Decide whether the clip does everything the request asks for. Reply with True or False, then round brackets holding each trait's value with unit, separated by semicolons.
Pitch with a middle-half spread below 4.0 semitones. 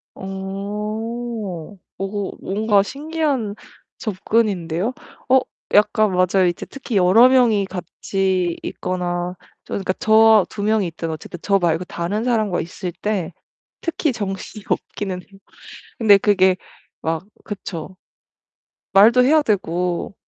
True (3.3 semitones)